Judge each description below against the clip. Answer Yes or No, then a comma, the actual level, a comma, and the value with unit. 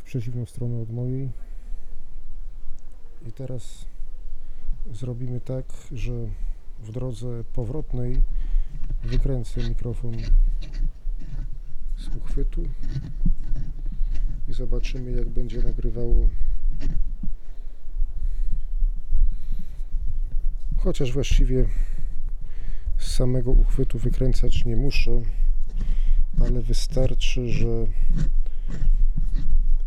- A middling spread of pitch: Yes, average, 3.8 semitones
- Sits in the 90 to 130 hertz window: Yes, low, 120 Hz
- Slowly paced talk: Yes, slow, 65 wpm